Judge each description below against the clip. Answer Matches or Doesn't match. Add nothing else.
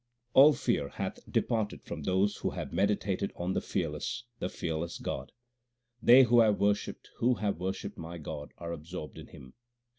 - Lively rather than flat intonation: Doesn't match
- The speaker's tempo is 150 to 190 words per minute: Matches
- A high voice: Doesn't match